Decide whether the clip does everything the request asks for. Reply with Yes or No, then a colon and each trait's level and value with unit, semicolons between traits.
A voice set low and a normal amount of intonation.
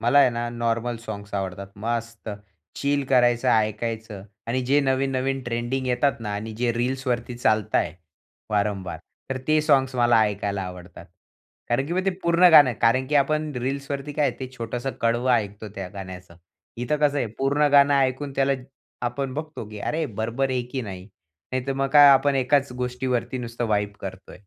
Yes: low, 125 Hz; average, 3.6 semitones